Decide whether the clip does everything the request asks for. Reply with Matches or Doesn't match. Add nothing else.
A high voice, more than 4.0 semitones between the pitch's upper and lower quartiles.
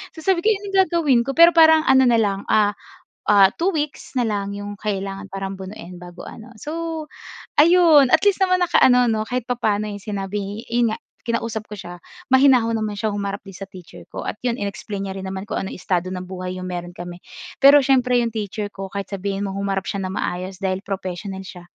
Matches